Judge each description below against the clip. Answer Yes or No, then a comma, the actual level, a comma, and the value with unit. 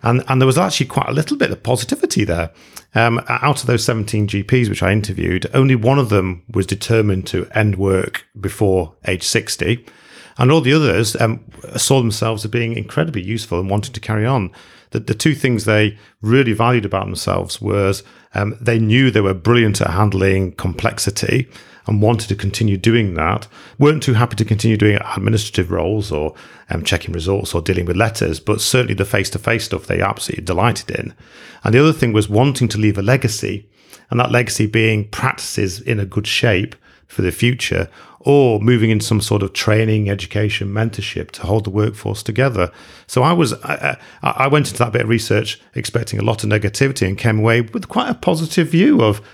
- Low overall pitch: Yes, low, 110 Hz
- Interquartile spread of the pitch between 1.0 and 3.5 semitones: Yes, average, 3.2 semitones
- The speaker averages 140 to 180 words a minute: No, average, 195 wpm